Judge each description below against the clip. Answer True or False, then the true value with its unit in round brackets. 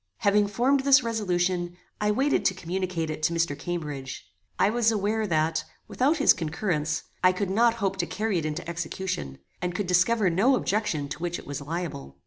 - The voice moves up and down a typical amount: True (4.5 semitones)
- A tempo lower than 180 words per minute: False (185 wpm)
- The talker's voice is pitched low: False (180 Hz)